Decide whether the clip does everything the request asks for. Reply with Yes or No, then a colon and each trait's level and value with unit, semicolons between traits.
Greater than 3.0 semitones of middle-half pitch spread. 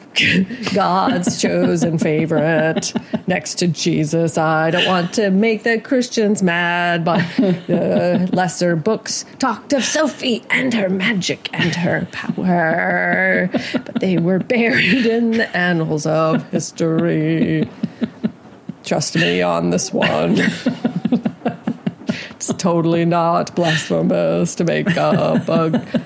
Yes: average, 4.9 semitones